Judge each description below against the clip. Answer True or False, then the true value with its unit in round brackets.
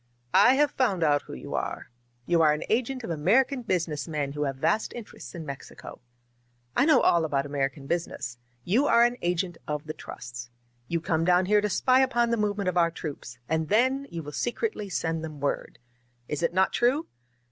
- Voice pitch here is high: False (170 Hz)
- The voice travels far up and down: True (7.7 semitones)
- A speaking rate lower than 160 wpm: False (205 wpm)